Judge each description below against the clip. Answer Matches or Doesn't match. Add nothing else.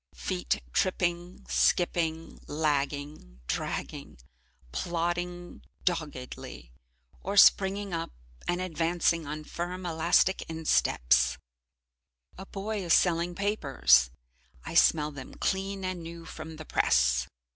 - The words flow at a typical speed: Doesn't match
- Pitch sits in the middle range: Matches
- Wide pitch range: Doesn't match